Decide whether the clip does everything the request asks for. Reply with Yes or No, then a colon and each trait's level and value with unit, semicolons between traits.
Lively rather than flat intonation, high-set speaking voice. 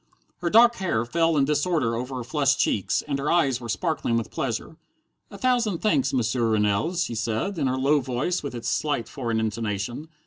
No: wide, 5.9 semitones; low, 135 Hz